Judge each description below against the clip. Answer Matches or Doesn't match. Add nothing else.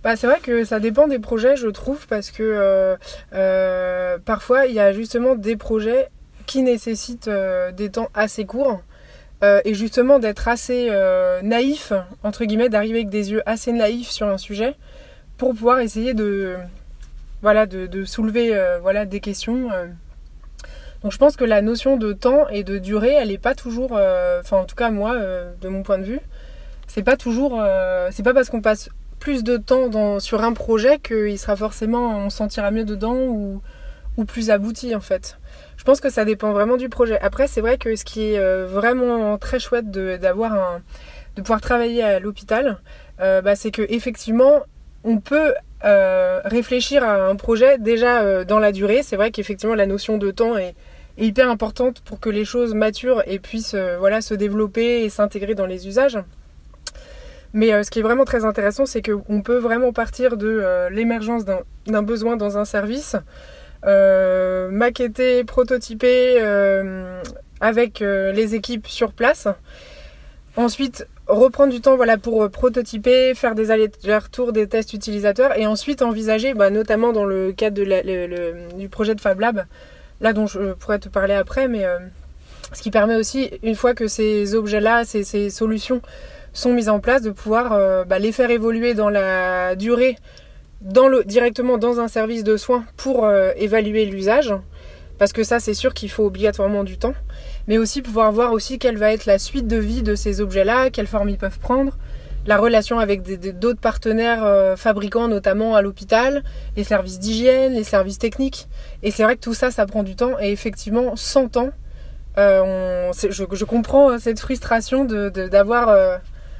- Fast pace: Doesn't match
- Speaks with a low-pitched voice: Doesn't match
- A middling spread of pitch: Matches